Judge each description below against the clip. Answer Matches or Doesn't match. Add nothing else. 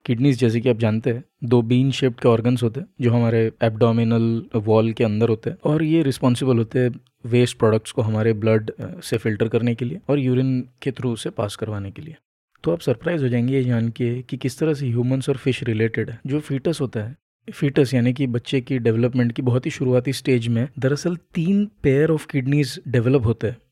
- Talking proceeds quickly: Matches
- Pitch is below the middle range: Matches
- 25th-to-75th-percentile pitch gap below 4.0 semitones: Matches